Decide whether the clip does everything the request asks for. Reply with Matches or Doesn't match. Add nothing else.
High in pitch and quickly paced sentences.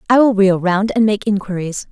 Matches